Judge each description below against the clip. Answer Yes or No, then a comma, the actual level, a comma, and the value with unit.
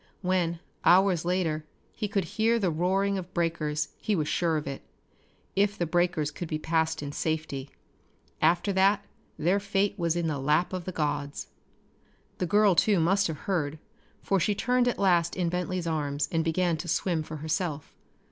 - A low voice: No, medium, 170 Hz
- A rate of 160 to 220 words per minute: Yes, average, 175 wpm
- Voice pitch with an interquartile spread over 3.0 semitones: Yes, average, 3.5 semitones